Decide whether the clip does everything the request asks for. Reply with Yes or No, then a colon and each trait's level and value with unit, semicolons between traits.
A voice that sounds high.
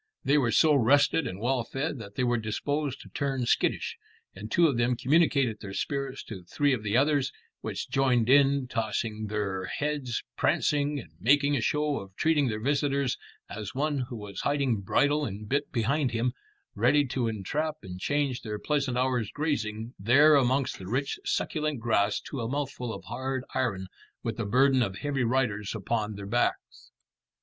No: low, 125 Hz